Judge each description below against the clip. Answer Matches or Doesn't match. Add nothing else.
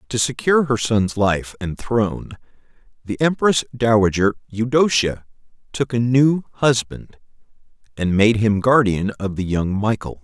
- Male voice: Matches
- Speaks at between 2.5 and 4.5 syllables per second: Matches